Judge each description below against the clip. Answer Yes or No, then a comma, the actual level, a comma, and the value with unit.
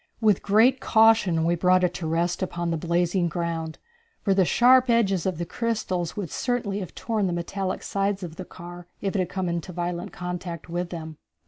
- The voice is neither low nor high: Yes, medium, 180 Hz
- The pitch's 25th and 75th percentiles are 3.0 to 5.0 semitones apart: No, narrow, 2.6 semitones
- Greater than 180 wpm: Yes, average, 200 wpm